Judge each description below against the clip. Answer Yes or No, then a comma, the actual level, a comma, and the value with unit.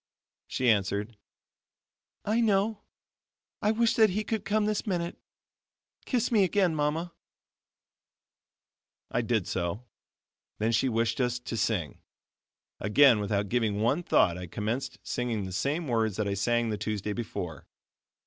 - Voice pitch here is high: No, low, 120 Hz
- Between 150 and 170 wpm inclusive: No, average, 140 wpm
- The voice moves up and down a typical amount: No, wide, 9.0 semitones